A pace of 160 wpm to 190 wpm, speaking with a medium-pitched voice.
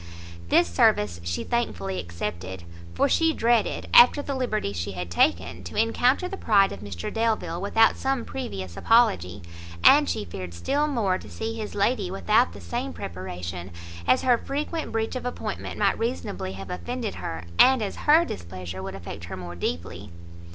Yes: average, 170 wpm; medium, 170 Hz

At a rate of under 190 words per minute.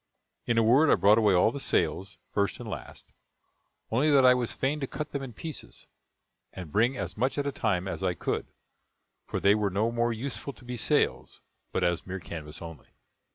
No: fast, 205 wpm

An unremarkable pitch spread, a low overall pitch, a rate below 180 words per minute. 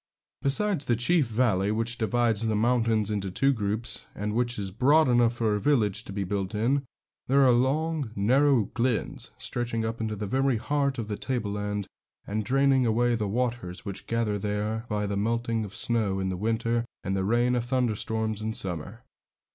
No: average, 3.0 semitones; low, 115 Hz; average, 185 wpm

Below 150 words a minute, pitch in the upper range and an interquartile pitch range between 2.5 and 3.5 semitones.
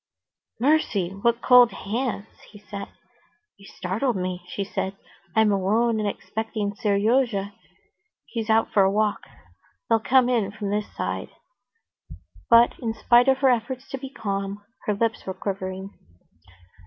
Yes: average, 140 wpm; high, 215 Hz; average, 3.1 semitones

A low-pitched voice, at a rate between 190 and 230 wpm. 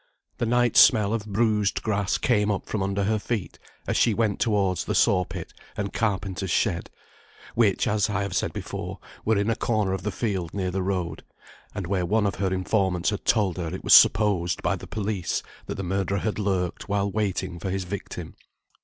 Yes: low, 100 Hz; average, 200 wpm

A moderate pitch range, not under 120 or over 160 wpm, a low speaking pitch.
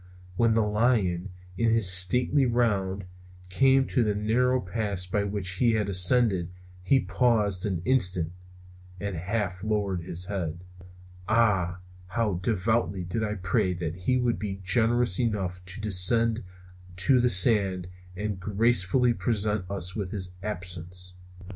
Yes: average, 3.9 semitones; average, 140 wpm; low, 100 Hz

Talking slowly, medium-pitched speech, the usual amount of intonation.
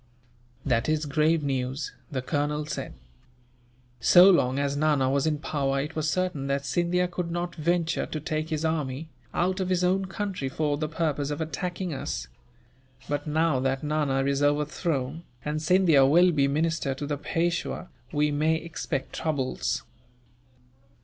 No: average, 155 wpm; medium, 150 Hz; average, 3.1 semitones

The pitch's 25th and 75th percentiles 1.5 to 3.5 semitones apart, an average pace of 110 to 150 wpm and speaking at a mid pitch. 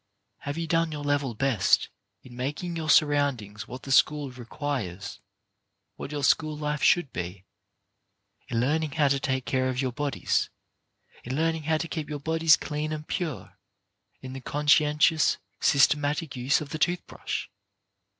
No: average, 3.1 semitones; average, 160 wpm; medium, 145 Hz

